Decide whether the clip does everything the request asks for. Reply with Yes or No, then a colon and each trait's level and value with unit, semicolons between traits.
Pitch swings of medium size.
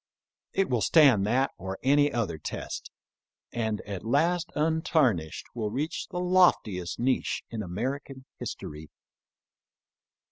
No: wide, 6.6 semitones